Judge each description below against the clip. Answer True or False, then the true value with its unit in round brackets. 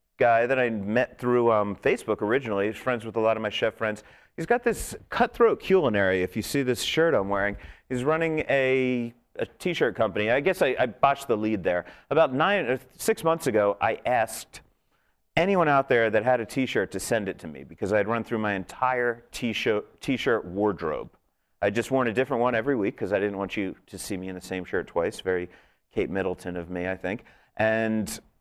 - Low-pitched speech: True (110 Hz)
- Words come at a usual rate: False (215 wpm)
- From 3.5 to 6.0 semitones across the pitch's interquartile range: True (4.4 semitones)